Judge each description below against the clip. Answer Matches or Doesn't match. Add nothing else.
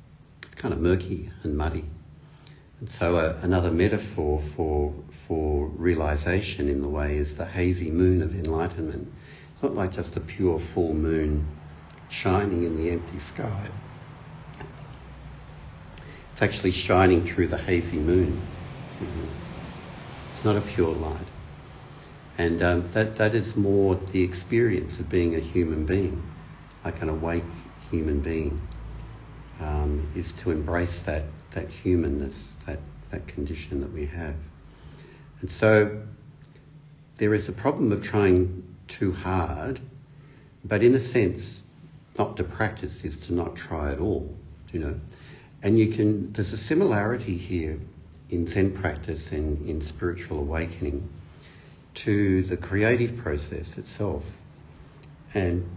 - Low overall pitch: Matches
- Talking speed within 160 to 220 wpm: Doesn't match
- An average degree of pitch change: Matches